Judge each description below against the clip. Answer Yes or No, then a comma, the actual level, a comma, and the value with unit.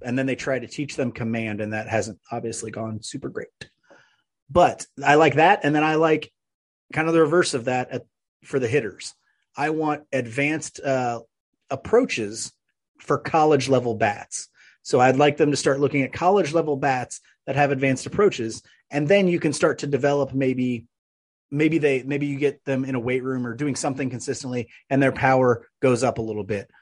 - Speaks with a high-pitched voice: No, low, 135 Hz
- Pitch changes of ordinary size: Yes, average, 3.3 semitones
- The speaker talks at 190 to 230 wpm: Yes, average, 195 wpm